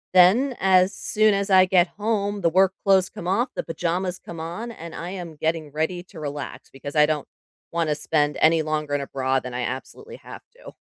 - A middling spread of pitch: Yes, average, 4.1 semitones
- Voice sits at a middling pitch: Yes, medium, 170 Hz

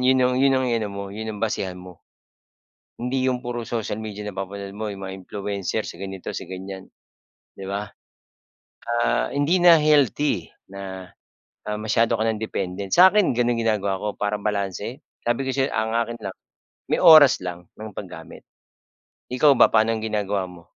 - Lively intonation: No, average, 3.8 semitones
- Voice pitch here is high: No, low, 105 Hz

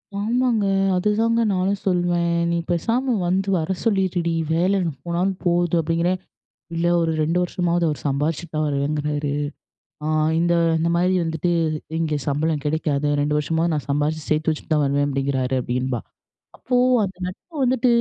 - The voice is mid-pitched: Yes, medium, 170 Hz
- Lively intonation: No, average, 3.7 semitones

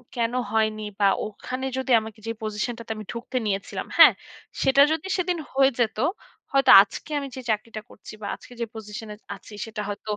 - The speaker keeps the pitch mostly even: No, average, 3.5 semitones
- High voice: Yes, high, 225 Hz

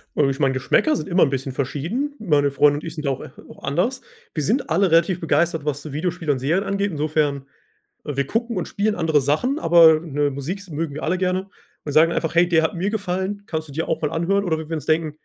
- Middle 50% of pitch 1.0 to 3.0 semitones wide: No, average, 4.2 semitones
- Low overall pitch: No, medium, 160 Hz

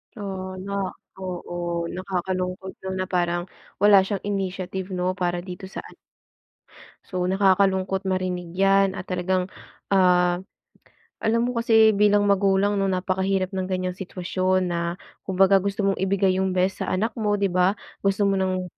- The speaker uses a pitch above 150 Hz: Yes, high, 190 Hz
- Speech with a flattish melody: Yes, narrow, 1.3 semitones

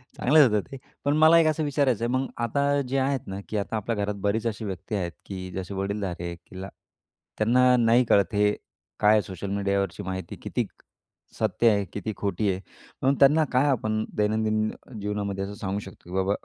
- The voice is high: No, low, 105 Hz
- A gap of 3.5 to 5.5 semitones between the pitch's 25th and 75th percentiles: Yes, average, 4.1 semitones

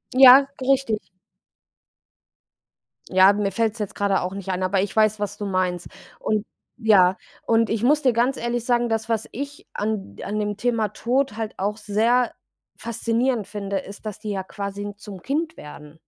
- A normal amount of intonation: Yes, average, 3.1 semitones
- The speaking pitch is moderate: No, high, 215 Hz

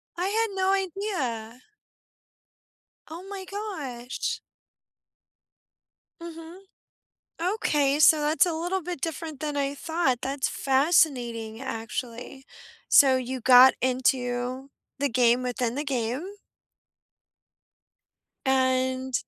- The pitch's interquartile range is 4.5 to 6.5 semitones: Yes, average, 4.8 semitones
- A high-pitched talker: Yes, very high, 270 Hz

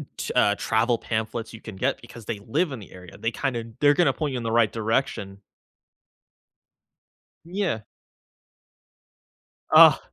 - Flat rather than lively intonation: No, average, 3.6 semitones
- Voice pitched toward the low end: Yes, low, 115 Hz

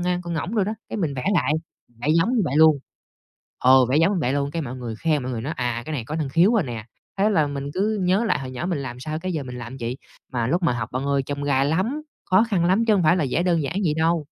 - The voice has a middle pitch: Yes, medium, 155 Hz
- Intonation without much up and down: No, wide, 5.4 semitones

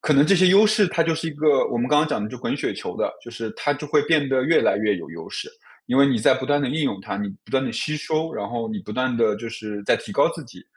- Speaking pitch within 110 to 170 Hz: Yes, low, 135 Hz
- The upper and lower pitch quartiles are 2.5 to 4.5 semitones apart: No, average, 5.3 semitones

